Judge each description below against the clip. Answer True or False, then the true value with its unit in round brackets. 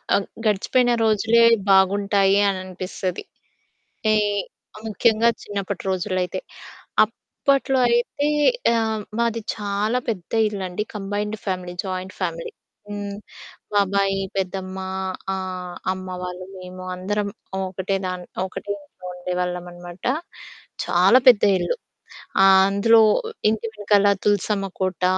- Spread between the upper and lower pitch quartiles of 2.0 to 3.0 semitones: True (2.4 semitones)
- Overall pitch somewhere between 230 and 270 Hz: False (195 Hz)